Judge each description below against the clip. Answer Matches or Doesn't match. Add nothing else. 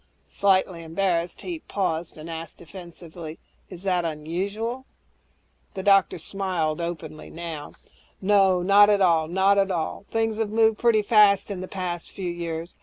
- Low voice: Doesn't match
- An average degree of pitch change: Matches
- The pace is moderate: Matches